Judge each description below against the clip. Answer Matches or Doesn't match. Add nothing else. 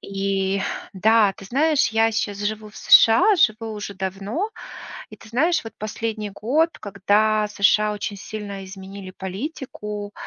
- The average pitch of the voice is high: Matches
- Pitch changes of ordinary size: Doesn't match